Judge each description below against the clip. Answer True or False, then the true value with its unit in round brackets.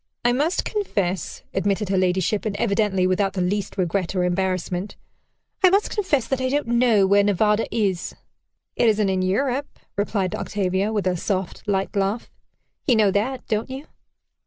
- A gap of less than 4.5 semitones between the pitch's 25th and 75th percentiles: True (3.8 semitones)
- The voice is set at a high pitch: True (205 Hz)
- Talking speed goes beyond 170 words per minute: False (165 wpm)